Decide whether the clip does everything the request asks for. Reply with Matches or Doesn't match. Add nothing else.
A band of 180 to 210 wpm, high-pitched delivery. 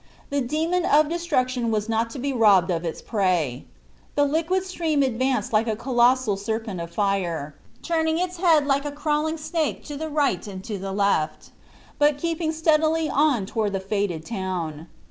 Doesn't match